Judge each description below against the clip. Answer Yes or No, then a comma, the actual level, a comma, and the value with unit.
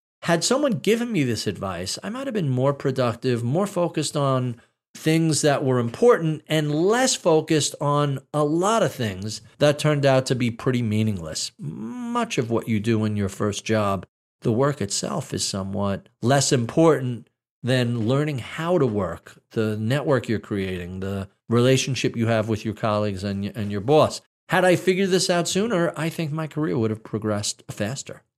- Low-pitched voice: Yes, low, 130 Hz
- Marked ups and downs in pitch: Yes, wide, 6.4 semitones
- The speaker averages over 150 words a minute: Yes, average, 175 wpm